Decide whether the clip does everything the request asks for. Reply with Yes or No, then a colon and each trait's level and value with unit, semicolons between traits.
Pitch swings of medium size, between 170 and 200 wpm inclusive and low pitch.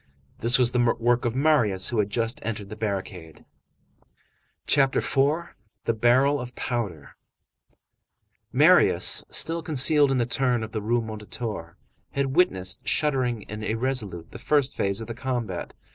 No: average, 3.9 semitones; average, 145 wpm; low, 120 Hz